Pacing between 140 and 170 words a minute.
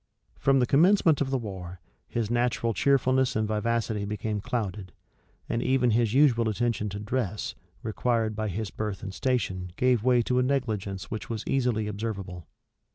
Yes: average, 160 wpm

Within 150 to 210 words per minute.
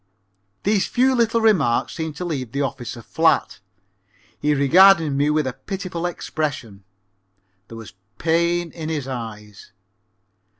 No: slow, 135 wpm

